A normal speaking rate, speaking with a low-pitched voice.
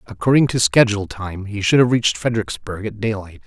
Yes: average, 190 wpm; low, 110 Hz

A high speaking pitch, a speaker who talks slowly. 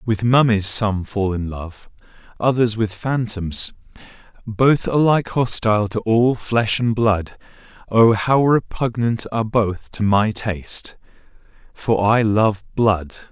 No: low, 110 Hz; slow, 125 wpm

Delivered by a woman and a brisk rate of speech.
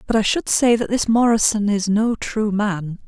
Yes: female; fast, 215 wpm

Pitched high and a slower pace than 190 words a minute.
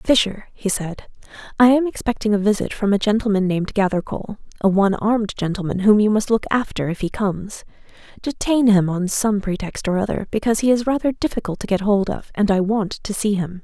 No: high, 205 Hz; average, 200 wpm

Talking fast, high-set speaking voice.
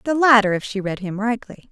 Yes: fast, 245 wpm; high, 220 Hz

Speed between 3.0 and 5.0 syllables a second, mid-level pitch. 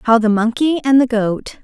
No: 4.6 syllables/s; high, 240 Hz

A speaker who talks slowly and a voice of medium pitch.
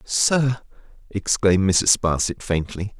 No: slow, 100 wpm; low, 105 Hz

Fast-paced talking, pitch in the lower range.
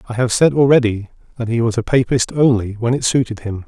Yes: fast, 230 wpm; low, 120 Hz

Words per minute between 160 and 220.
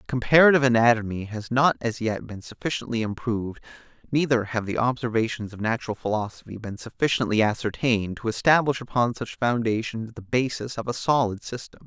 No: average, 150 wpm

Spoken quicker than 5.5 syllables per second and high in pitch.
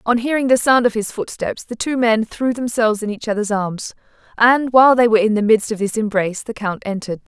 Yes: 6.0 syllables/s; high, 225 Hz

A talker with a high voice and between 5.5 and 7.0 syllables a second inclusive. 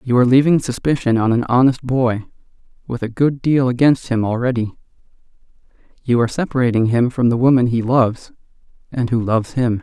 No: low, 125 Hz; 5.9 syllables/s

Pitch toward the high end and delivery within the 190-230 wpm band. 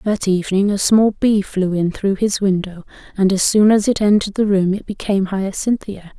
Yes: high, 200 Hz; fast, 205 wpm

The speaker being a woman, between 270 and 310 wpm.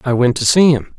No: male; fast, 305 wpm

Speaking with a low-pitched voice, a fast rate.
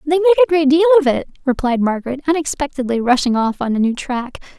No: very high, 280 Hz; fast, 210 wpm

